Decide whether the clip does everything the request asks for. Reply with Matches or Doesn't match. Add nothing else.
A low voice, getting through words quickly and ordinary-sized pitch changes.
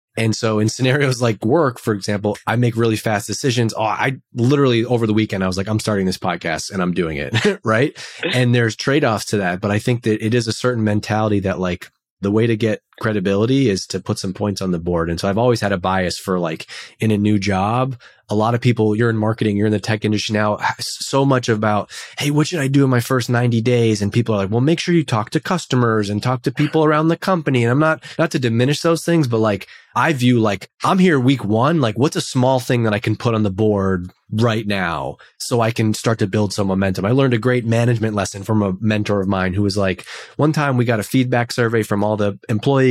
Matches